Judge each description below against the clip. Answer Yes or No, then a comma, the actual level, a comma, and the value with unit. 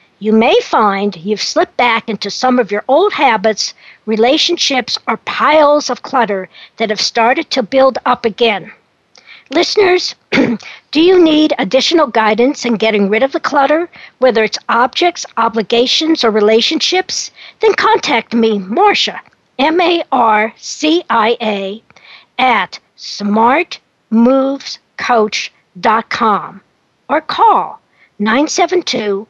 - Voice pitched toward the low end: No, high, 245 Hz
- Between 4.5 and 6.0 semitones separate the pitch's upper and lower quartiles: Yes, wide, 5.6 semitones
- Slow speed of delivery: Yes, slow, 120 wpm